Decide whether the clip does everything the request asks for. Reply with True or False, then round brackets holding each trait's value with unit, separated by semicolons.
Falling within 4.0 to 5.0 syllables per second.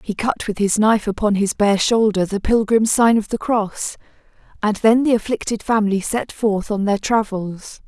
True (4.9 syllables/s)